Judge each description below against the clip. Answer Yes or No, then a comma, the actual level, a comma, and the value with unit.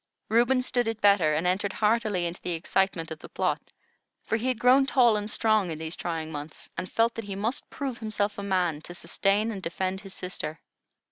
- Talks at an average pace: No, fast, 210 wpm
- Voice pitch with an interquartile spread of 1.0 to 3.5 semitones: No, average, 4.5 semitones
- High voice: Yes, high, 200 Hz